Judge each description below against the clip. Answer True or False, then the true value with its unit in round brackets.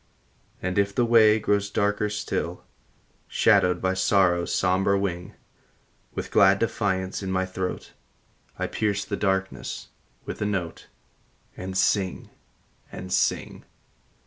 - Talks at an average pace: False (125 wpm)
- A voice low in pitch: True (95 Hz)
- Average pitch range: False (1.6 semitones)